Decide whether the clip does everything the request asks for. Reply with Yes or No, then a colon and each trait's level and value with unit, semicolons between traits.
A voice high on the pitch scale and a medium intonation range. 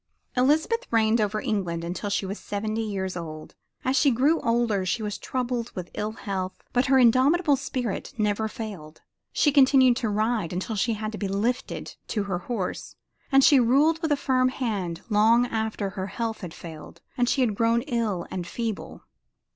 Yes: high, 220 Hz; average, 4.2 semitones